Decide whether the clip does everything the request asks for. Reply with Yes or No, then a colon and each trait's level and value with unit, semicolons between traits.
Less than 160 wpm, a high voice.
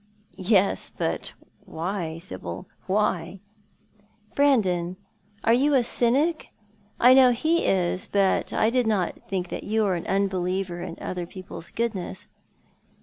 Yes: average, 140 wpm; high, 195 Hz